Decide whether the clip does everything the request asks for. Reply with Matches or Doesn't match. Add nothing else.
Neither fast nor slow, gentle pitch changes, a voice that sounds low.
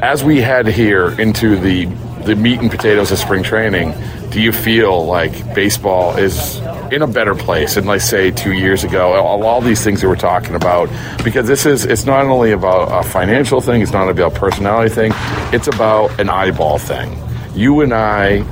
Doesn't match